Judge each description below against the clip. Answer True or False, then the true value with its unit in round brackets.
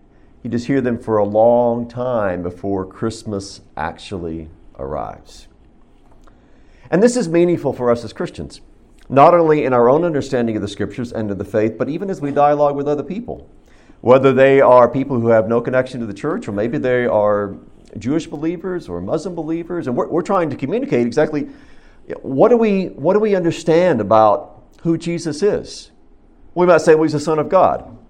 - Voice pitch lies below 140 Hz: True (130 Hz)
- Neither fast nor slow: True (190 wpm)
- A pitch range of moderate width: False (6.9 semitones)